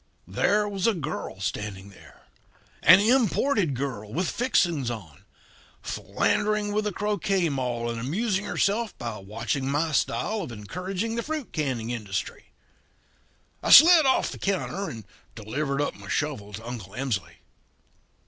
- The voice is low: No, medium, 150 Hz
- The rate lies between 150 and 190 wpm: No, average, 140 wpm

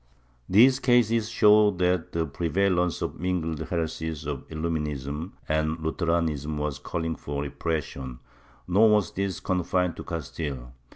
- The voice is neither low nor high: No, very low, 80 Hz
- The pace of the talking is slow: Yes, slow, 130 wpm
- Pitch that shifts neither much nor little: Yes, average, 3.5 semitones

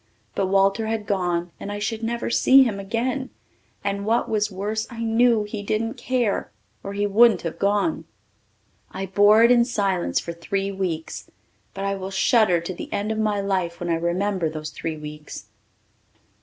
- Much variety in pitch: No, average, 3.1 semitones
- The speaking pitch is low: No, high, 200 Hz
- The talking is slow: No, average, 180 wpm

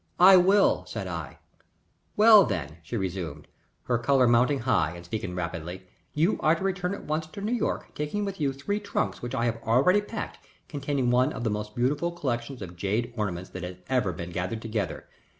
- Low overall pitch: Yes, low, 120 Hz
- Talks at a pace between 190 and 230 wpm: Yes, average, 195 wpm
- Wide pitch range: Yes, wide, 8.5 semitones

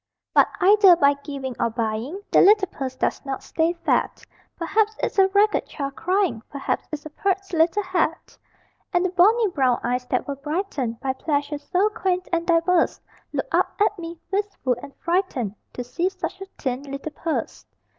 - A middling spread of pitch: No, wide, 5.8 semitones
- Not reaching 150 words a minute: No, average, 175 wpm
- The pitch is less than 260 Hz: No, very high, 335 Hz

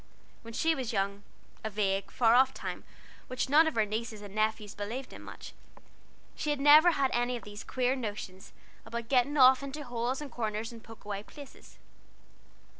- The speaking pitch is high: Yes, high, 235 Hz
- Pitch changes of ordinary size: Yes, average, 3.9 semitones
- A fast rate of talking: No, average, 185 wpm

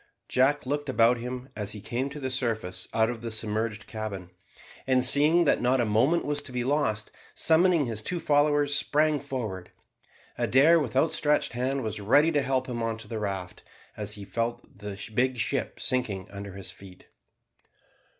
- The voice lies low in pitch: Yes, low, 125 Hz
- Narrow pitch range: No, average, 4.9 semitones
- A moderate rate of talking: Yes, average, 180 wpm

